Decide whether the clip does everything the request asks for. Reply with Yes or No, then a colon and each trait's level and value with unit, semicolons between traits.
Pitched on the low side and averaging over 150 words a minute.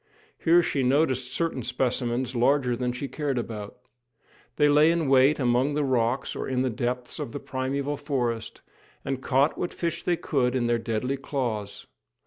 Yes: low, 130 Hz; average, 170 wpm